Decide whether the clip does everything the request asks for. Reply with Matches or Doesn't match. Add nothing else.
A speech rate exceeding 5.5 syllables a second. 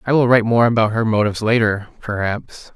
Matches